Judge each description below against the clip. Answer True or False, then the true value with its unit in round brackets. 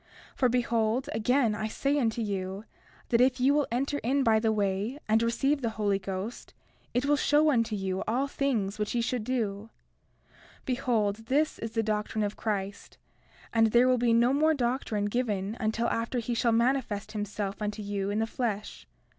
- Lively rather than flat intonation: False (3.2 semitones)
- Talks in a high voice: True (225 Hz)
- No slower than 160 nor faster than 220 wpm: True (190 wpm)